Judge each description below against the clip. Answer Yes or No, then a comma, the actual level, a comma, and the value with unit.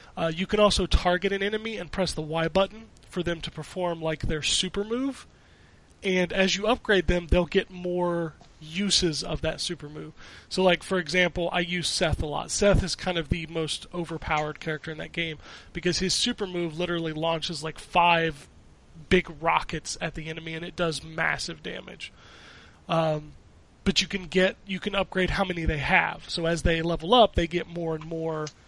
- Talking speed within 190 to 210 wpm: Yes, average, 195 wpm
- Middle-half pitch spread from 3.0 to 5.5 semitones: No, narrow, 2.5 semitones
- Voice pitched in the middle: Yes, medium, 175 Hz